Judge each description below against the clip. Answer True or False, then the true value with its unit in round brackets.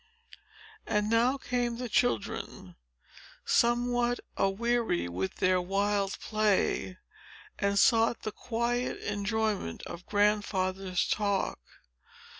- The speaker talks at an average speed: False (90 wpm)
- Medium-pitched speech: False (210 Hz)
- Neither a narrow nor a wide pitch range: True (3.6 semitones)